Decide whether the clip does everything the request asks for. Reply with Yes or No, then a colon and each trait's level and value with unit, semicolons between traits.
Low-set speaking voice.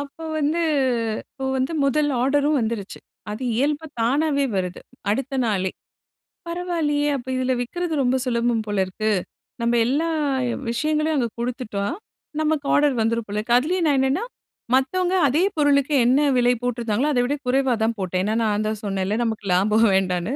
No: very high, 255 Hz